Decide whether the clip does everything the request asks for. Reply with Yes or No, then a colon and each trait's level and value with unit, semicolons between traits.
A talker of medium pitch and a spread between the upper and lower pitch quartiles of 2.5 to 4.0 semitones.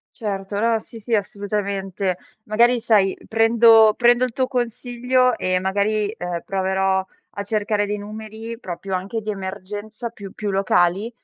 No: high, 210 Hz; average, 2.8 semitones